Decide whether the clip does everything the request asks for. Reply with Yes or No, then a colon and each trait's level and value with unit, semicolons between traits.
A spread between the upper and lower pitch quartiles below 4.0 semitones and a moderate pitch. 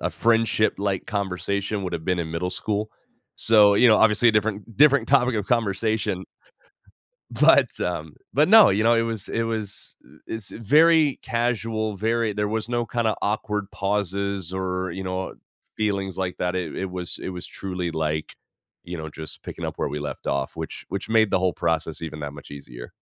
No: average, 3.6 semitones; low, 100 Hz